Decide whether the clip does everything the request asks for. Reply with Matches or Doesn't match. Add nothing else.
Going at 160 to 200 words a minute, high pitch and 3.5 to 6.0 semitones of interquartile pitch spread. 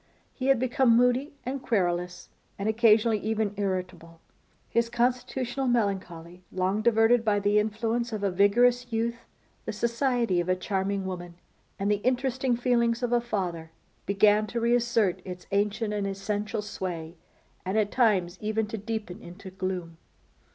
Doesn't match